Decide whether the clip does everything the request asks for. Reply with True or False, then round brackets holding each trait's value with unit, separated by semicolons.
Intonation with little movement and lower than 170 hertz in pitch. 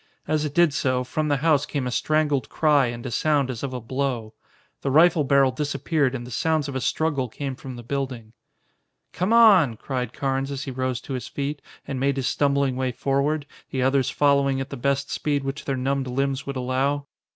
True (1.9 semitones; 140 Hz)